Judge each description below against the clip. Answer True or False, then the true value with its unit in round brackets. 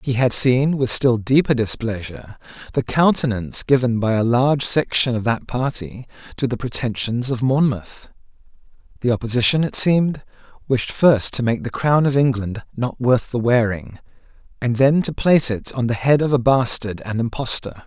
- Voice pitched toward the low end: True (125 Hz)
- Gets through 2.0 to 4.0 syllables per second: False (5.0 syllables/s)